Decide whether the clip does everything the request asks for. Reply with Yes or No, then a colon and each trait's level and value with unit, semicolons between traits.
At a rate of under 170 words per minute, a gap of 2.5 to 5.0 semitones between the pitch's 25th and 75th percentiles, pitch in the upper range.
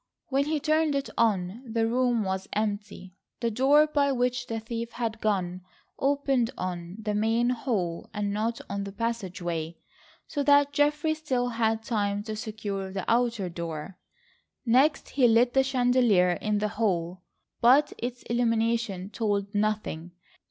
Yes: average, 150 wpm; average, 3.8 semitones; high, 225 Hz